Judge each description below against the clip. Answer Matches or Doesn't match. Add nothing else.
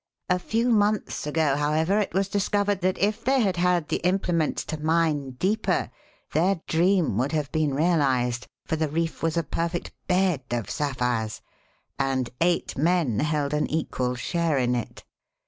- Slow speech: Doesn't match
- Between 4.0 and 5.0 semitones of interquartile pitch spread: Matches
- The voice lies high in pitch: Doesn't match